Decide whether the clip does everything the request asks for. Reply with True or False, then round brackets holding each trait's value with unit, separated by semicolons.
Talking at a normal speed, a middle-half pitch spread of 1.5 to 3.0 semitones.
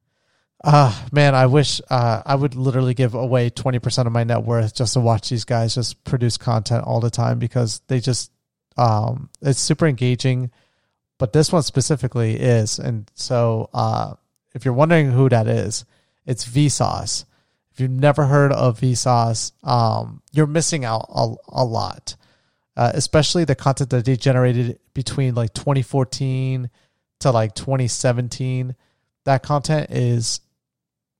True (155 wpm; 2.5 semitones)